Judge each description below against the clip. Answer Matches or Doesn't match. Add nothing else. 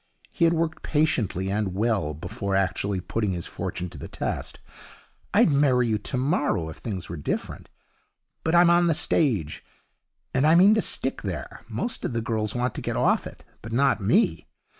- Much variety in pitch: Matches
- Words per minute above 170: Matches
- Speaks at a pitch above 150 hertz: Doesn't match